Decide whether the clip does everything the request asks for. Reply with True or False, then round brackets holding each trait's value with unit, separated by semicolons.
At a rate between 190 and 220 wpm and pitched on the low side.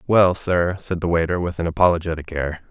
True (200 wpm; 85 Hz)